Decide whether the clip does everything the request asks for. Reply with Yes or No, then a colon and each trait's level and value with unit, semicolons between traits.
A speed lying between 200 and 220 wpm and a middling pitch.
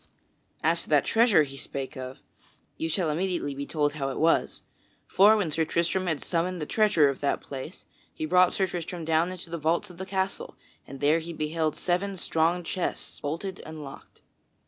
No: average, 190 wpm; medium, 165 Hz